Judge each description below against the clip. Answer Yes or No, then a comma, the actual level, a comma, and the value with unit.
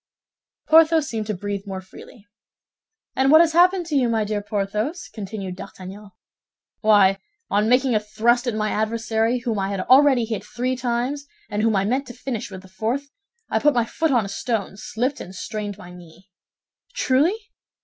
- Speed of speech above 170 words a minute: Yes, average, 180 wpm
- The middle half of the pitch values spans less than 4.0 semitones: No, average, 4.3 semitones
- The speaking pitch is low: No, high, 220 Hz